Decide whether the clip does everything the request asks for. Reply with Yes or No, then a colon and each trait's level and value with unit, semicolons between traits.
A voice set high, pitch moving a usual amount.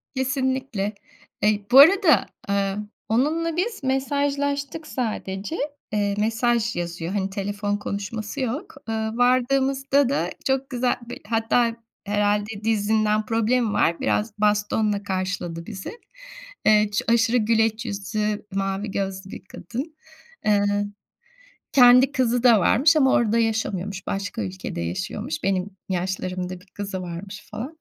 Yes: high, 215 Hz; average, 4.2 semitones